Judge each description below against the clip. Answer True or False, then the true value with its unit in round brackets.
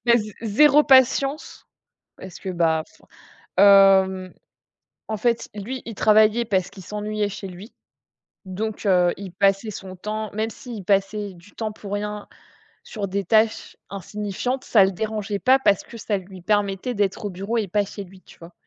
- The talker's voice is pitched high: True (205 Hz)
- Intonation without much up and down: True (2.2 semitones)